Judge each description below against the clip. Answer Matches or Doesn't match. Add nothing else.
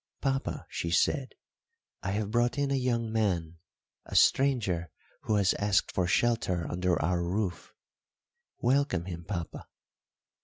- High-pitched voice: Doesn't match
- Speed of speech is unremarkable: Doesn't match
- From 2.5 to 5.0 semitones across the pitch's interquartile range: Doesn't match